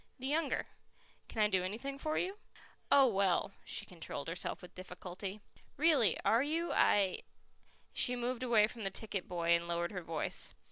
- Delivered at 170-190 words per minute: Yes, average, 175 wpm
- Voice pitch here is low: No, high, 210 Hz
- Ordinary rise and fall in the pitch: No, wide, 6.1 semitones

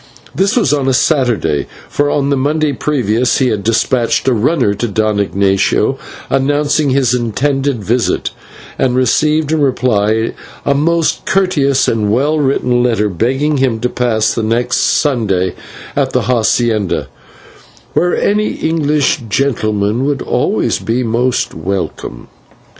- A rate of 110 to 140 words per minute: Yes, slow, 135 wpm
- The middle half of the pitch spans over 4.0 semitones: Yes, average, 4.7 semitones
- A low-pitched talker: Yes, low, 125 Hz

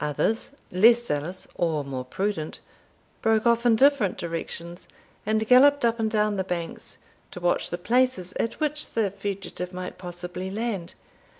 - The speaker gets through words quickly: No, average, 155 wpm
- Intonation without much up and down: No, average, 4.7 semitones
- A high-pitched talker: Yes, high, 200 Hz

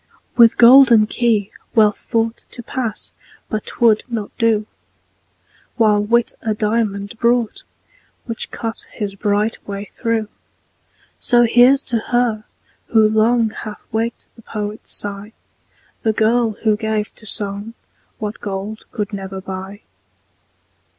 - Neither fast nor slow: No, slow, 125 wpm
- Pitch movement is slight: Yes, narrow, 1.9 semitones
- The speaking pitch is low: No, high, 220 Hz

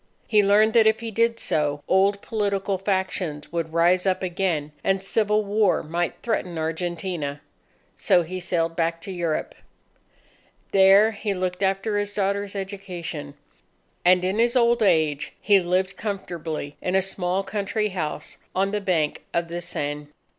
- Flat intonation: No, average, 3.2 semitones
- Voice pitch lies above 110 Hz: Yes, high, 190 Hz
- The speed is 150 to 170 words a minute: Yes, average, 155 wpm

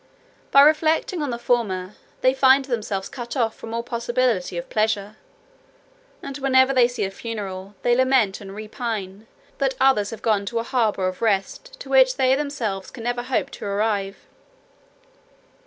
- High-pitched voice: Yes, high, 235 Hz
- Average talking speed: Yes, average, 165 wpm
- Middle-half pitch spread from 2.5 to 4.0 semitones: No, average, 4.4 semitones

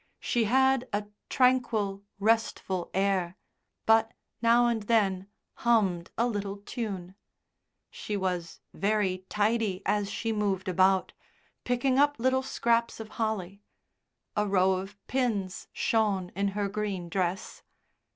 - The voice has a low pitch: No, high, 205 Hz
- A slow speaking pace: Yes, slow, 120 wpm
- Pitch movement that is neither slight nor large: Yes, average, 3.3 semitones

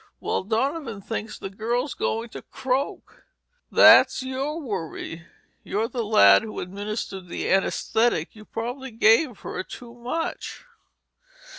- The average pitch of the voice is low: No, high, 225 Hz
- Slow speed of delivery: Yes, slow, 125 wpm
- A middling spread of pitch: Yes, average, 4.2 semitones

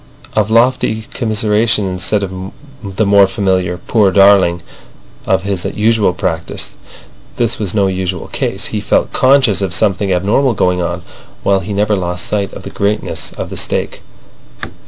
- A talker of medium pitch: No, low, 100 Hz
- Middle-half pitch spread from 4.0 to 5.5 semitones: No, narrow, 2.5 semitones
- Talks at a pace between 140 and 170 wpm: Yes, average, 155 wpm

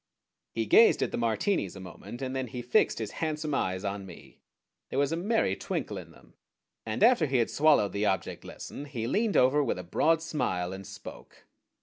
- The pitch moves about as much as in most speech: No, wide, 7.4 semitones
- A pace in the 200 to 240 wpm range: Yes, fast, 205 wpm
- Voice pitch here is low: Yes, low, 125 Hz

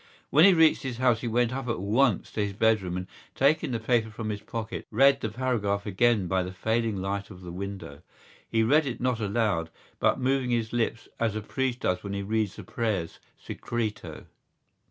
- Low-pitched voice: Yes, low, 110 Hz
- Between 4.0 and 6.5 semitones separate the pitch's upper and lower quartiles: No, average, 3.5 semitones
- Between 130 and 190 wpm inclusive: No, average, 200 wpm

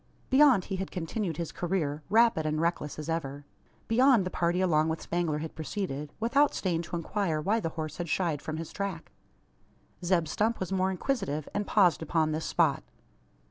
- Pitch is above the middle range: No, medium, 170 Hz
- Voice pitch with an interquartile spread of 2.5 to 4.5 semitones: Yes, average, 3.9 semitones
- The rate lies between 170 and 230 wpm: Yes, average, 180 wpm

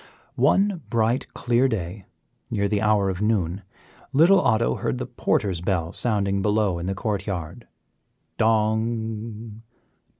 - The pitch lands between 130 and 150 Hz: No, low, 105 Hz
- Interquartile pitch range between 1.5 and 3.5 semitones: Yes, average, 2.9 semitones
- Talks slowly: Yes, slow, 130 wpm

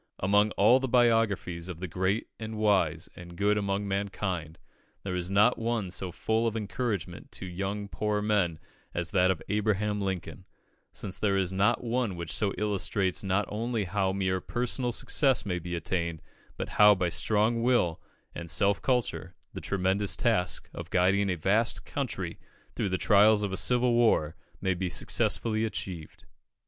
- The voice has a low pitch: Yes, low, 100 Hz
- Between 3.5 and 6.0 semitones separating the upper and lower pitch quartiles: No, average, 2.9 semitones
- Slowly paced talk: No, average, 165 wpm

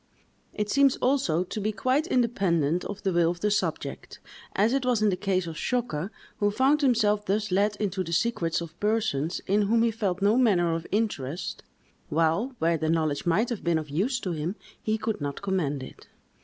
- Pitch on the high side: Yes, high, 200 Hz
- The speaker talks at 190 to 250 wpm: Yes, average, 200 wpm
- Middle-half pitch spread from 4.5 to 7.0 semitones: Yes, average, 5.0 semitones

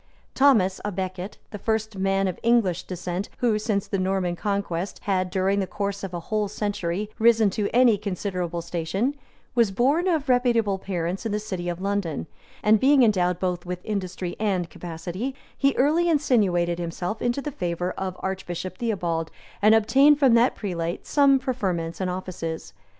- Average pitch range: Yes, average, 4.1 semitones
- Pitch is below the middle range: No, high, 195 Hz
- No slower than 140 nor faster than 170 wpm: Yes, average, 165 wpm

